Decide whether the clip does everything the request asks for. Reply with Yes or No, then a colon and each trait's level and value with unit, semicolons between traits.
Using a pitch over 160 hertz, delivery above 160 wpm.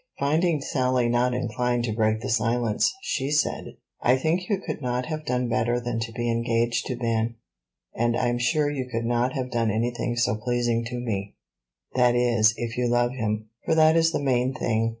No: low, 120 Hz; average, 195 wpm